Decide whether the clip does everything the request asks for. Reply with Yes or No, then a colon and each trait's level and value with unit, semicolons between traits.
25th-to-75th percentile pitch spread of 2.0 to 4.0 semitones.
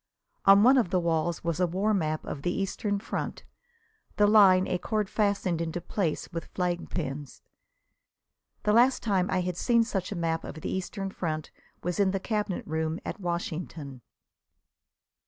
Yes: average, 3.4 semitones